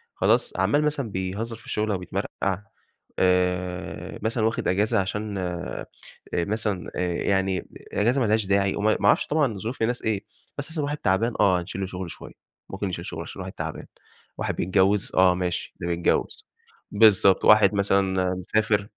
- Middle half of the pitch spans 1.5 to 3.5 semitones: Yes, average, 3.0 semitones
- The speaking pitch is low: Yes, low, 100 Hz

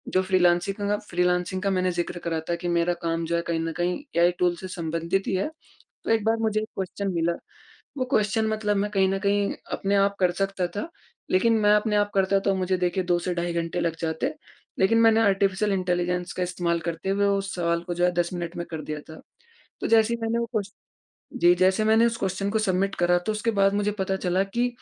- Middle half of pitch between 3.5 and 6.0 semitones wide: No, average, 2.8 semitones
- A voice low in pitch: No, high, 190 Hz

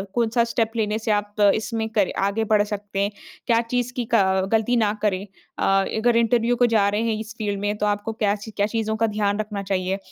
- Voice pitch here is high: Yes, high, 215 Hz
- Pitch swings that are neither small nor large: No, narrow, 1.8 semitones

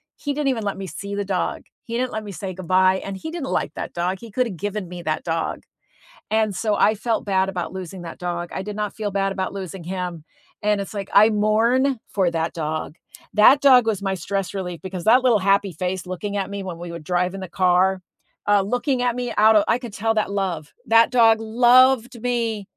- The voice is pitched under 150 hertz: No, high, 200 Hz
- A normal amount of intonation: Yes, average, 3.3 semitones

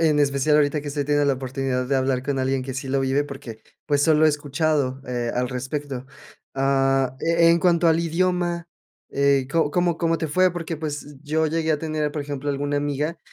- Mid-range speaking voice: Yes, medium, 145 Hz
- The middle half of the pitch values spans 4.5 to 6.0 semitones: No, average, 2.9 semitones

